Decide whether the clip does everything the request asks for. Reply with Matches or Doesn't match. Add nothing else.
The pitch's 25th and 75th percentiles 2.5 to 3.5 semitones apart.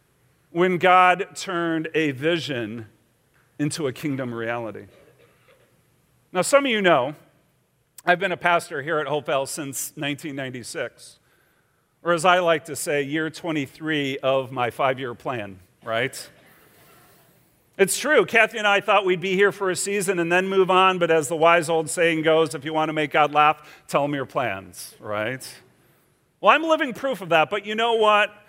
Doesn't match